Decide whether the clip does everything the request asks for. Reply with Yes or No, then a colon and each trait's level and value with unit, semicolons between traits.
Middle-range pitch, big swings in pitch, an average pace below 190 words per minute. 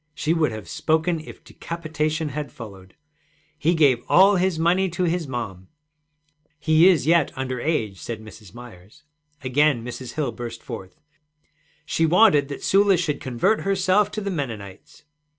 Yes: medium, 150 Hz; wide, 6.2 semitones; average, 150 wpm